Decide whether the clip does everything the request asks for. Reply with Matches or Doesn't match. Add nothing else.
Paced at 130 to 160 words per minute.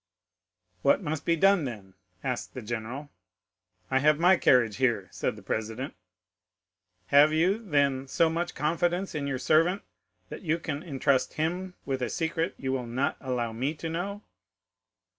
Matches